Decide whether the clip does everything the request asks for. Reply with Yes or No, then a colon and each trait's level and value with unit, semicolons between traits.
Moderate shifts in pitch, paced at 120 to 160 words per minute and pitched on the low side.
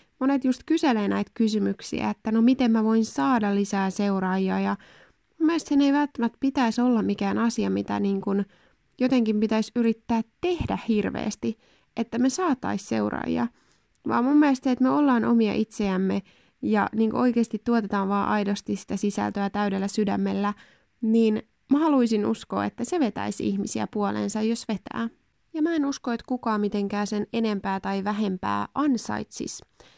No: average, 3.7 semitones; fast, 155 wpm; high, 220 Hz